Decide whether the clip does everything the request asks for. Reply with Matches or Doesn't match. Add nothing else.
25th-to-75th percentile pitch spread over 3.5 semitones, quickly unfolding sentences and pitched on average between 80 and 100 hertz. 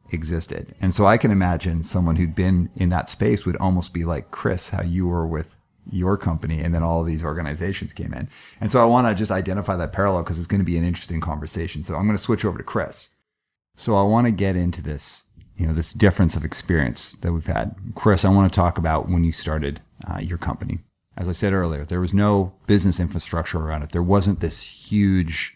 Doesn't match